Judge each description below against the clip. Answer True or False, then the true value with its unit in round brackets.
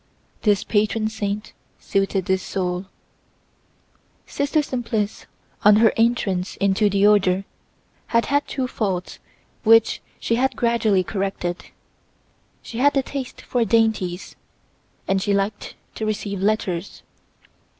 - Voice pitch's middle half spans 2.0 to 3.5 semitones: True (3.0 semitones)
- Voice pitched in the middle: False (210 Hz)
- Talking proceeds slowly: True (120 wpm)